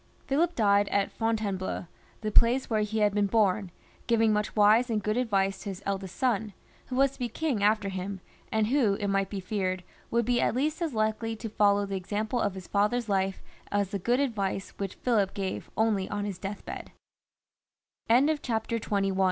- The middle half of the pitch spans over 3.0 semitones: No, narrow, 2.6 semitones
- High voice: Yes, high, 210 Hz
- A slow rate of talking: No, average, 175 wpm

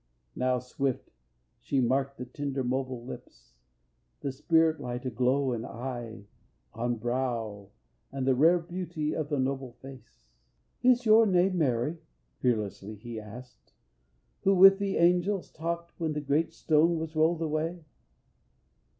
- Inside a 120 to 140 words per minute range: Yes, slow, 135 wpm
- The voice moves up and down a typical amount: Yes, average, 5.0 semitones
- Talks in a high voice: No, low, 135 Hz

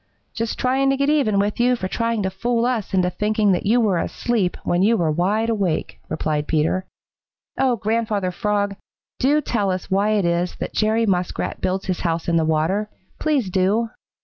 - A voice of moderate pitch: No, high, 205 Hz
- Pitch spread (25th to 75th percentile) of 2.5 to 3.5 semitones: No, average, 4.1 semitones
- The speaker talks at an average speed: Yes, average, 190 wpm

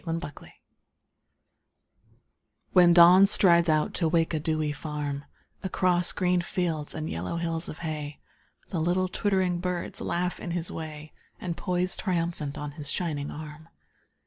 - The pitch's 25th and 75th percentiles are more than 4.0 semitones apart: No, narrow, 2.6 semitones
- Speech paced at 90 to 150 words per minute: Yes, average, 145 wpm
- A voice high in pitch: No, medium, 170 Hz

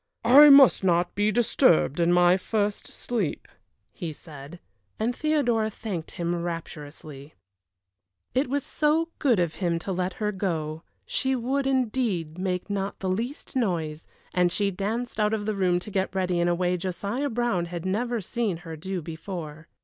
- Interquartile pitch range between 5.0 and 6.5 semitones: Yes, average, 5.3 semitones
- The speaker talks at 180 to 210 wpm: No, average, 165 wpm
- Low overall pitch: No, high, 190 Hz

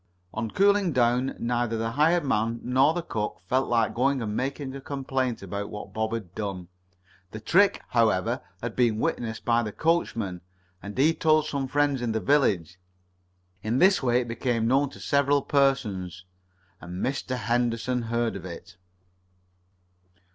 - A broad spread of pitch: No, average, 4.0 semitones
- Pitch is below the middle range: Yes, low, 120 Hz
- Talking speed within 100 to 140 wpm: No, average, 160 wpm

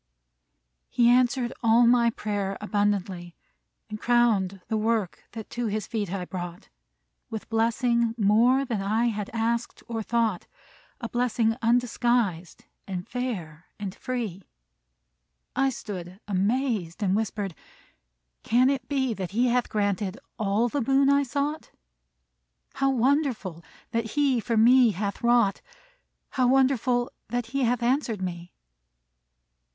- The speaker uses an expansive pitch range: No, average, 3.4 semitones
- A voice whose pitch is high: Yes, high, 230 Hz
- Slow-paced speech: Yes, slow, 130 wpm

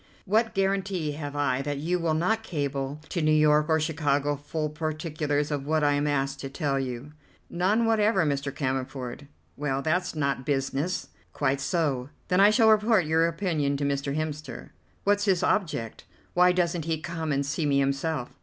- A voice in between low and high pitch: Yes, medium, 150 Hz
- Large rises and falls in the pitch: No, average, 3.9 semitones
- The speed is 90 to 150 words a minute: No, average, 175 wpm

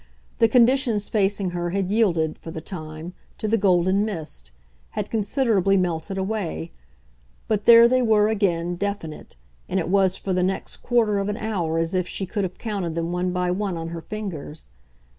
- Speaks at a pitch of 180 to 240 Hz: Yes, high, 190 Hz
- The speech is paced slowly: No, average, 180 wpm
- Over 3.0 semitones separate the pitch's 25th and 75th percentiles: Yes, average, 3.7 semitones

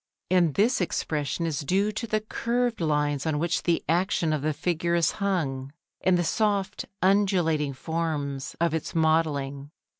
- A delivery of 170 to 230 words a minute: No, average, 155 wpm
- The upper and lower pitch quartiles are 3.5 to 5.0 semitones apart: Yes, average, 4.2 semitones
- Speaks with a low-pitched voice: No, medium, 165 Hz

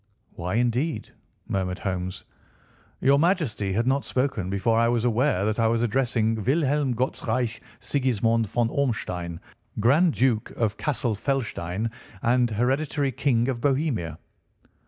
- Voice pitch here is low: Yes, low, 120 Hz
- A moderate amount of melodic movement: Yes, average, 3.9 semitones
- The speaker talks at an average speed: No, slow, 130 wpm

